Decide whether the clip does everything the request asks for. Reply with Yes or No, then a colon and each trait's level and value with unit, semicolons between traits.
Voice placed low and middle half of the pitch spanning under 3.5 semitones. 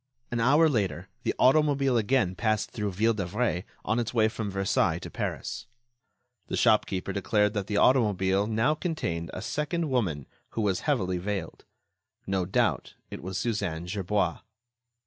No: low, 105 Hz; average, 4.4 semitones